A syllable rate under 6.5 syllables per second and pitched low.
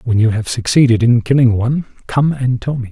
Yes: 5.8 syllables/s; low, 120 Hz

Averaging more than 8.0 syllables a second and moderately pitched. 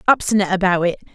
No: 8.2 syllables/s; high, 195 Hz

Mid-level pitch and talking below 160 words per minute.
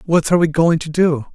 No: medium, 165 Hz; fast, 270 wpm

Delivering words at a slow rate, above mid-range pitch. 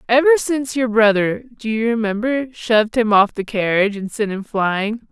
No: average, 190 wpm; high, 225 Hz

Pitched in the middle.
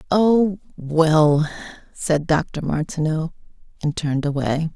Yes: medium, 160 Hz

